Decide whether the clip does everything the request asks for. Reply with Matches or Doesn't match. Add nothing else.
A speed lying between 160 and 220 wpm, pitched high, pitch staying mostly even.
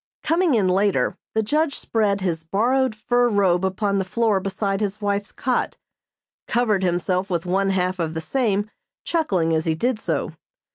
Doesn't match